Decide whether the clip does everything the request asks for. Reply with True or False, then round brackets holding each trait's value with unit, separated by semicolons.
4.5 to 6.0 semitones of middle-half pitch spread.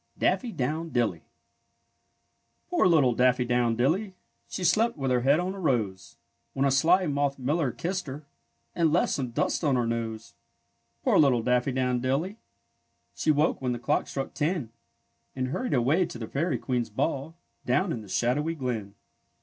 True (5.0 semitones)